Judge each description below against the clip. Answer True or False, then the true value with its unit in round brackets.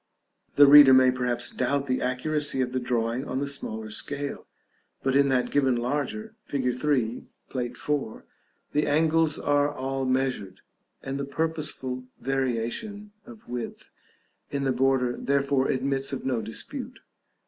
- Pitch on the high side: False (135 Hz)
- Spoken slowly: False (145 wpm)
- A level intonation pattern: True (2.2 semitones)